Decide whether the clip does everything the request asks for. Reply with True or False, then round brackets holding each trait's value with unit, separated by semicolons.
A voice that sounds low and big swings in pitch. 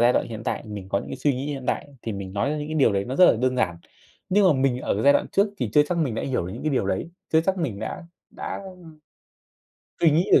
True (130 Hz; 6.3 semitones)